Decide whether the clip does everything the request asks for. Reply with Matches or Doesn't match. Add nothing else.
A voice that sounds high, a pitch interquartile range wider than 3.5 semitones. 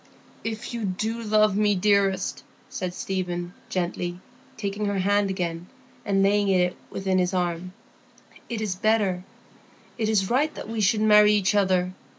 Doesn't match